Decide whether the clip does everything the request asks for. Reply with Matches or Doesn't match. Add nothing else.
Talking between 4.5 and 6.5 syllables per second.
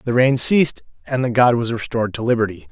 Matches